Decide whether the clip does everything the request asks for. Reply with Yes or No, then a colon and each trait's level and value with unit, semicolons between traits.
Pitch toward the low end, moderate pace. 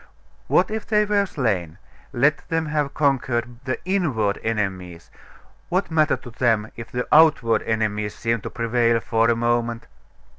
Yes: low, 120 Hz; average, 150 wpm